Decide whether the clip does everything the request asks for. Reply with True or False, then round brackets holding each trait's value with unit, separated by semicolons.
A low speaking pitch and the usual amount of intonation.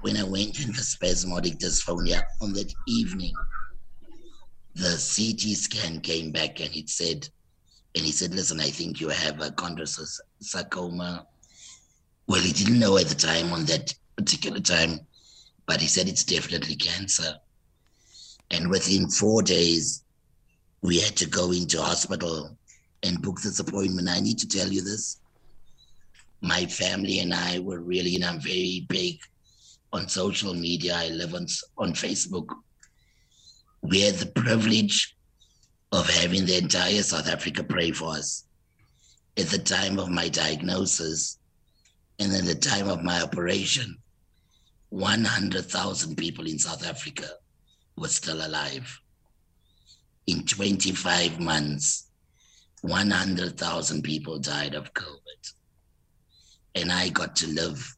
True (90 Hz; 3.0 semitones)